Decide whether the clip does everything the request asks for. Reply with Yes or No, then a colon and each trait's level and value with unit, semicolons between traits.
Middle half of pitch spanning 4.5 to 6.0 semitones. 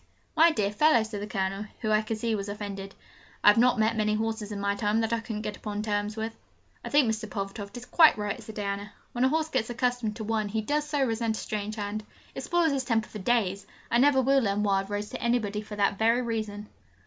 No: narrow, 2.5 semitones